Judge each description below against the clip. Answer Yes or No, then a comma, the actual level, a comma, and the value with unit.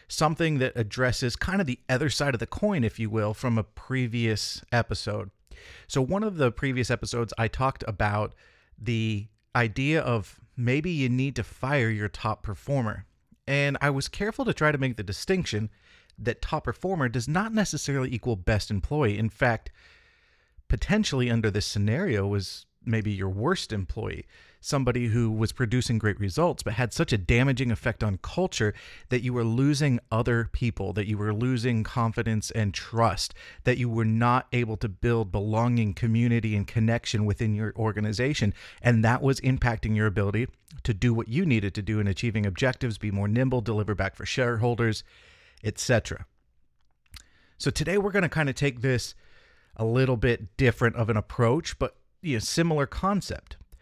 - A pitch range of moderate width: Yes, average, 3.4 semitones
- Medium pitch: No, low, 115 Hz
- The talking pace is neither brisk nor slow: Yes, average, 175 wpm